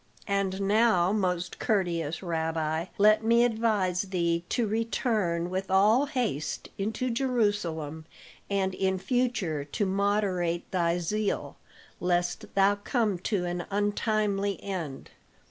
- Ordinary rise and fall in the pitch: Yes, average, 3.5 semitones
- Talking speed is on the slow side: Yes, slow, 115 wpm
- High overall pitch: Yes, high, 195 Hz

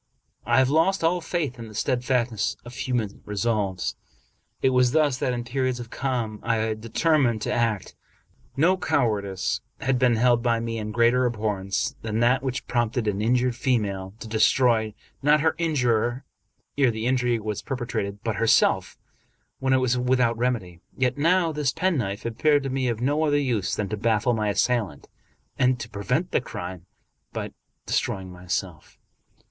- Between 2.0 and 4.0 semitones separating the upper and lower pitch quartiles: Yes, average, 3.3 semitones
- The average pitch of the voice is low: Yes, low, 120 Hz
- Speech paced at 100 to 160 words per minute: No, average, 170 wpm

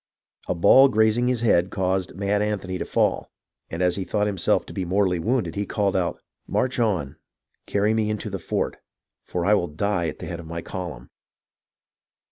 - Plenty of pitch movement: No, average, 3.3 semitones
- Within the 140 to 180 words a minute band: No, average, 195 wpm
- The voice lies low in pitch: Yes, very low, 95 Hz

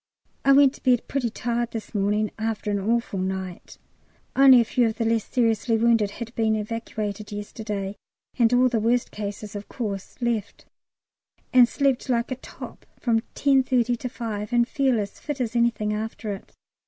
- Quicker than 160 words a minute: Yes, average, 175 wpm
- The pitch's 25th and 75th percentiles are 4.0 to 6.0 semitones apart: No, narrow, 2.6 semitones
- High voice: Yes, high, 230 Hz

